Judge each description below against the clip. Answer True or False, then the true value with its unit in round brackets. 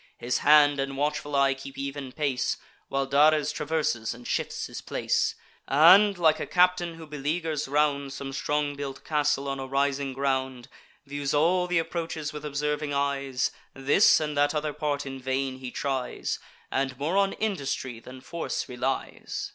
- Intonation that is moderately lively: False (2.0 semitones)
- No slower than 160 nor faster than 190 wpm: True (165 wpm)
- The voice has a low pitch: False (145 Hz)